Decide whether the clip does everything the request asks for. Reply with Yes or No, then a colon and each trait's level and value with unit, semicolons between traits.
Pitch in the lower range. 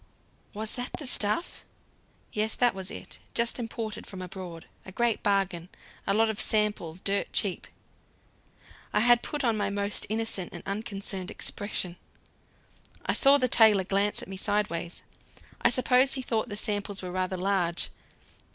No: high, 205 Hz